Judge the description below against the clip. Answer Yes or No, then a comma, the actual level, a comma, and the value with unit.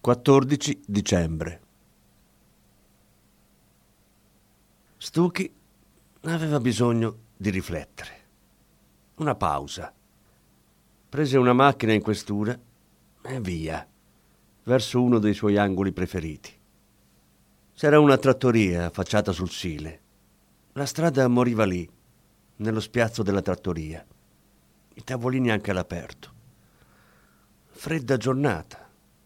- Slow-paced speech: Yes, slow, 85 wpm